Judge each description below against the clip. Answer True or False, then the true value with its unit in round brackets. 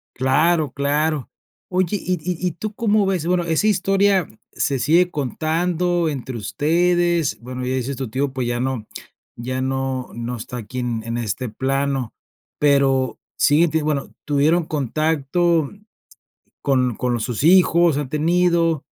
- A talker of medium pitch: True (145 Hz)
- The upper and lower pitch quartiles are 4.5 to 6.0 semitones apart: True (4.9 semitones)